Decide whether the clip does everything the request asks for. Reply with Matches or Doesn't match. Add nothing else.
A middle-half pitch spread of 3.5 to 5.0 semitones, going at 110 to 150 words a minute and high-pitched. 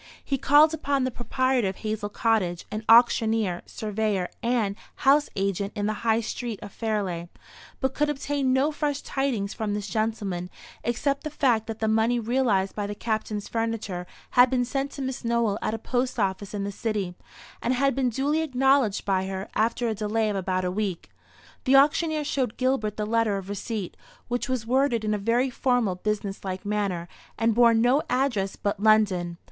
Doesn't match